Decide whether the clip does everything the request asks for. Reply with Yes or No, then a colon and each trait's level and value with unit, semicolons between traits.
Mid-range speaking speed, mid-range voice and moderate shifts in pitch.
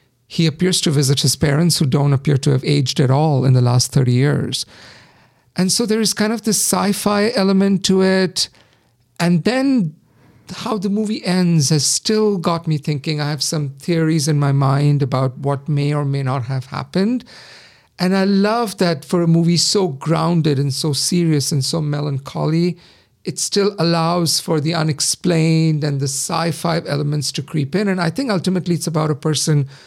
Yes: average, 190 wpm; medium, 160 Hz; average, 4.4 semitones